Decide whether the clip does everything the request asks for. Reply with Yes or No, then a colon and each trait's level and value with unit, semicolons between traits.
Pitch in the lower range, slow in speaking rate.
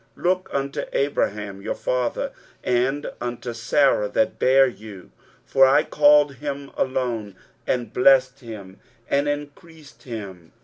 Yes: low, 130 Hz; slow, 130 wpm